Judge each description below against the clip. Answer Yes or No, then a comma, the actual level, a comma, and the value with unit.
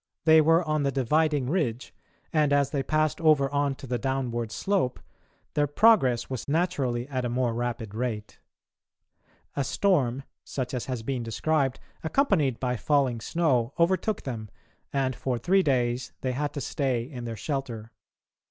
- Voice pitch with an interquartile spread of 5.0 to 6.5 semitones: No, average, 4.0 semitones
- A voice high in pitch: No, low, 135 Hz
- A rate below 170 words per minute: Yes, average, 160 wpm